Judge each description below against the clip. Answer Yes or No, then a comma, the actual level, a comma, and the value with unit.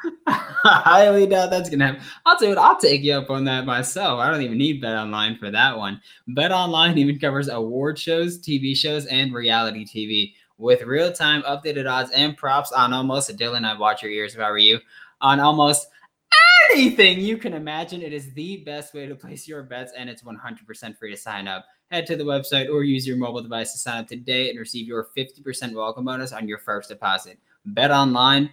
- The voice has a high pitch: No, medium, 140 Hz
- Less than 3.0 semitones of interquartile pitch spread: No, average, 4.4 semitones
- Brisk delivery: Yes, fast, 215 wpm